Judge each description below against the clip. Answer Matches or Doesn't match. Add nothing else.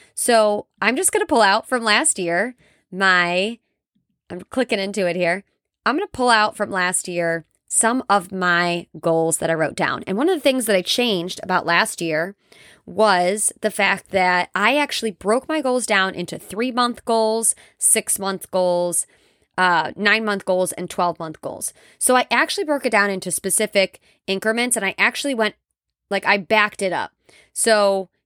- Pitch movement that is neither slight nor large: Matches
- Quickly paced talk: Doesn't match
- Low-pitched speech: Doesn't match